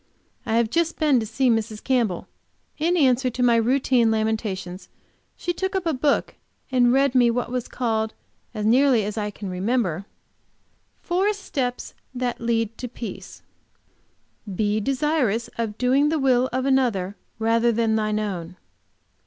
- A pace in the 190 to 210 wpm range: No, average, 155 wpm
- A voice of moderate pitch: No, high, 235 Hz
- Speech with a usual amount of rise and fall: Yes, average, 3.3 semitones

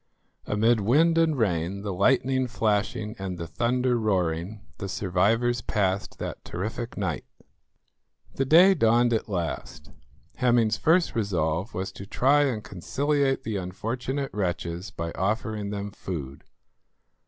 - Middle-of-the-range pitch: No, low, 105 Hz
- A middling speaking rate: No, slow, 130 wpm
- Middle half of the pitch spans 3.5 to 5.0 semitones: Yes, average, 4.7 semitones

